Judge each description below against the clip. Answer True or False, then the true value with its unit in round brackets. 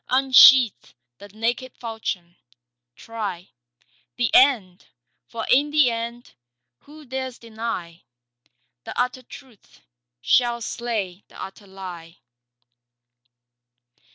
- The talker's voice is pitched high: True (230 Hz)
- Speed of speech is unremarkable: False (95 wpm)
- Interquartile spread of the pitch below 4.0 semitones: False (4.8 semitones)